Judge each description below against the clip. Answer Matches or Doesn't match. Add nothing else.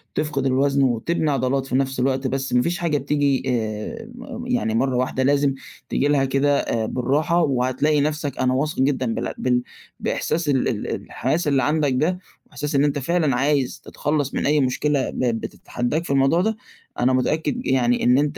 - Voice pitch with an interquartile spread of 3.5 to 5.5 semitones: Doesn't match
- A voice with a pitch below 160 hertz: Matches